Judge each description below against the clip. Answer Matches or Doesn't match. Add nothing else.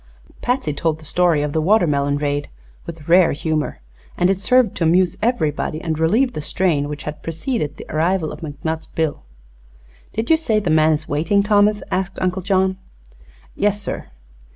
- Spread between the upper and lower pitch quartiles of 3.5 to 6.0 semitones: Matches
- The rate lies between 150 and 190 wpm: Matches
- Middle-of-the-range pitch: Matches